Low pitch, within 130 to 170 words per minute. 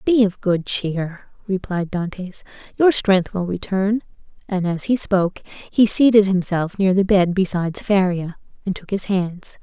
No: high, 190 Hz; average, 160 wpm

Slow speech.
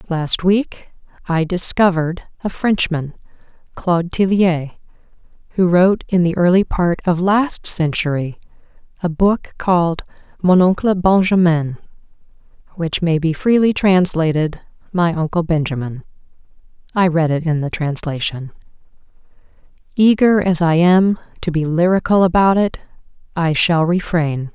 Yes: slow, 120 wpm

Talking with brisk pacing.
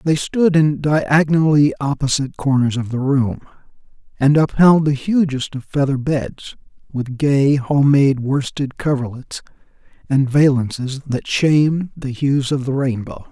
No: slow, 135 wpm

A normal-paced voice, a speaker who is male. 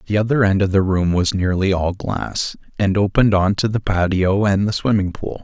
No: fast, 210 wpm; male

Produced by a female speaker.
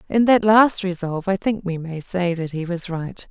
Yes: female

